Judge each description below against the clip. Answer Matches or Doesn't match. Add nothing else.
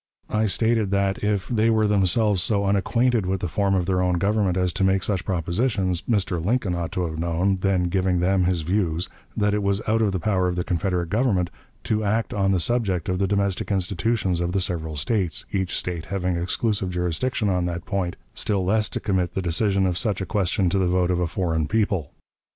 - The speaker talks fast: Matches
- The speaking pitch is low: Matches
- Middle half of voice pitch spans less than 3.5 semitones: Matches